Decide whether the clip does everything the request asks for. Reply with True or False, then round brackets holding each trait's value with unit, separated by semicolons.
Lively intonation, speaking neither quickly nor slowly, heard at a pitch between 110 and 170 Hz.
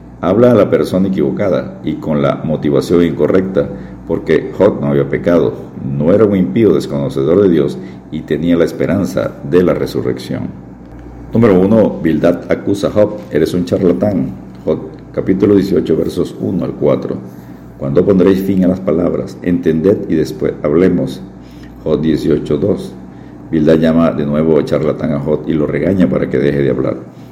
False (5.9 semitones; 165 wpm; 75 Hz)